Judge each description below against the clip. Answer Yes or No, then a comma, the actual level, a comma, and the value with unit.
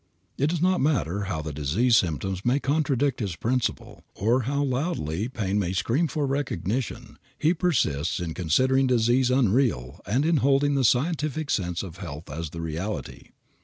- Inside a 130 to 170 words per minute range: Yes, average, 165 wpm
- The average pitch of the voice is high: No, low, 120 Hz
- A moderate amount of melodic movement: No, wide, 7.8 semitones